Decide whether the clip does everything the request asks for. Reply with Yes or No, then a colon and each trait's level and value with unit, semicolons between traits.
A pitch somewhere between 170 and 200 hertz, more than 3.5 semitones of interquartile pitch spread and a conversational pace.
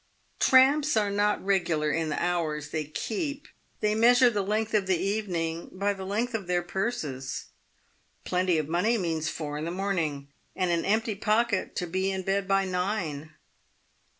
Yes: high, 190 Hz; average, 4.3 semitones; average, 170 wpm